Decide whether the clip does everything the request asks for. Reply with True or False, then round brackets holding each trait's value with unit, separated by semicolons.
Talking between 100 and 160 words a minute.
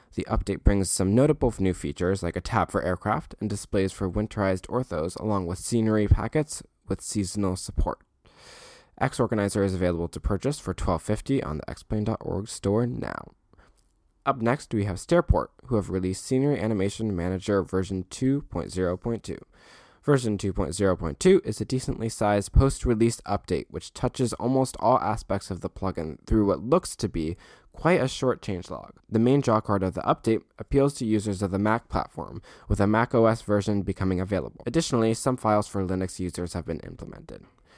False (175 wpm)